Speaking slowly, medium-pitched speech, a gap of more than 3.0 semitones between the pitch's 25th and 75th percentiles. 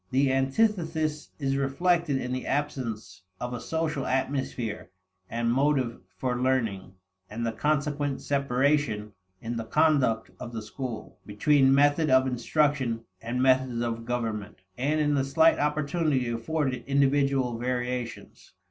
No: slow, 130 wpm; low, 130 Hz; average, 3.6 semitones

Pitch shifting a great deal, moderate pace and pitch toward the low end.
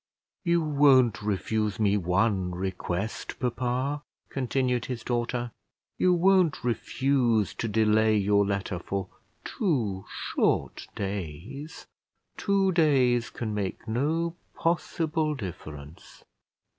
No: wide, 6.0 semitones; slow, 100 wpm; low, 120 Hz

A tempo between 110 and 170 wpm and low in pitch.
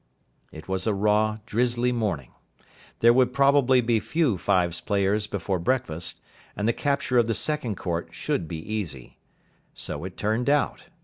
Yes: average, 160 wpm; low, 110 Hz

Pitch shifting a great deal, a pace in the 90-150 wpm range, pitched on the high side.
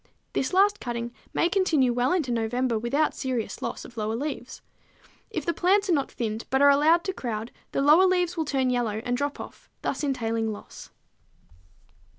No: wide, 5.7 semitones; average, 180 wpm; very high, 265 Hz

